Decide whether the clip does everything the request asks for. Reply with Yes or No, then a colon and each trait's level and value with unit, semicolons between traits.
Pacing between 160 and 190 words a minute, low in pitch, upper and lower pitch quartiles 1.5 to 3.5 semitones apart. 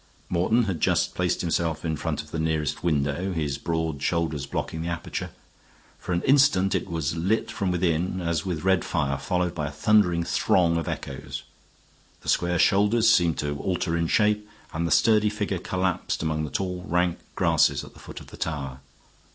Yes: average, 185 wpm; very low, 85 Hz; average, 2.9 semitones